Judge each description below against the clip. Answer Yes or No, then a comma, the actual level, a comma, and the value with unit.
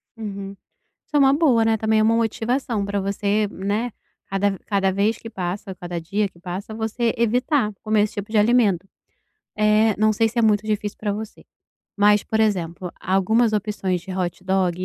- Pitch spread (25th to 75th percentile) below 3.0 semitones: Yes, narrow, 2.4 semitones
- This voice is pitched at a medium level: No, high, 210 Hz